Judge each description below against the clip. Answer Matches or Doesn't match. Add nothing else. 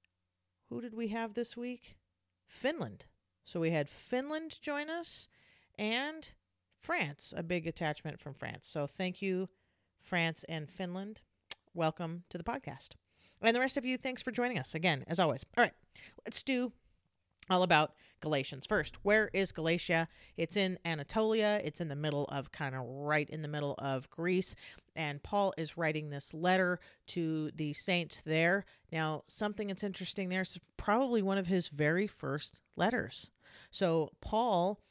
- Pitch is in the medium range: Matches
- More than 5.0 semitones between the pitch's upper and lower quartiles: Matches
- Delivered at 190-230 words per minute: Doesn't match